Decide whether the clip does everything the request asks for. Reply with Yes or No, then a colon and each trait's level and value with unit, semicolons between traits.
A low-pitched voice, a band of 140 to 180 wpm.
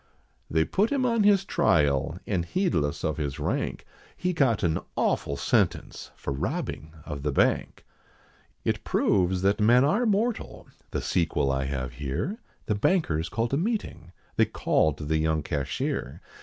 Yes: very low, 85 Hz; average, 155 wpm